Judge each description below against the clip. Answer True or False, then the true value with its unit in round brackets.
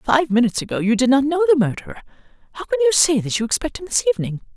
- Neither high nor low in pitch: False (265 Hz)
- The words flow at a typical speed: False (250 wpm)